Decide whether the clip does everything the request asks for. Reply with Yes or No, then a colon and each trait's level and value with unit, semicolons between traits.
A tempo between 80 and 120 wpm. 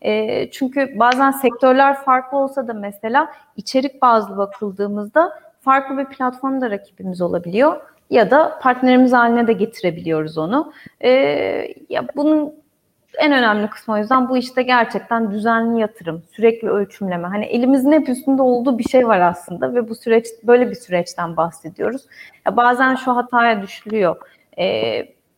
No: average, 135 wpm